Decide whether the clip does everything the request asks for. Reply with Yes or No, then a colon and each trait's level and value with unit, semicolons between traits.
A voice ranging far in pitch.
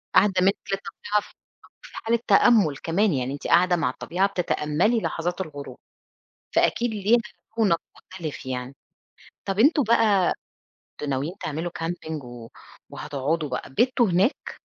Yes: wide, 5.9 semitones